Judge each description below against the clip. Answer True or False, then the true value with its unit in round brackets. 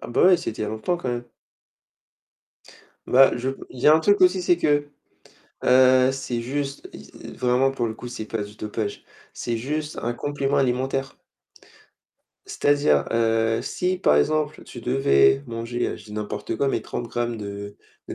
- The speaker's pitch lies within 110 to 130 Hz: True (125 Hz)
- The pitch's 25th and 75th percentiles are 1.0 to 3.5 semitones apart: False (4.1 semitones)